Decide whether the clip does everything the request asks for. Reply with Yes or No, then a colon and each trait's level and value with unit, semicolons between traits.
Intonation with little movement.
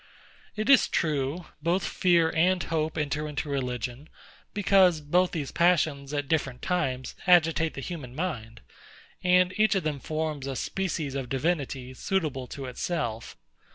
No: average, 4.6 semitones